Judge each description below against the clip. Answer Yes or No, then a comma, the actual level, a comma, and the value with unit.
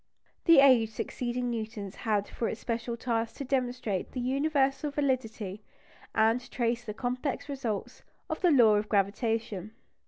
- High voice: Yes, high, 235 Hz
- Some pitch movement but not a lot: Yes, average, 3.2 semitones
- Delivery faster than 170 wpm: No, average, 145 wpm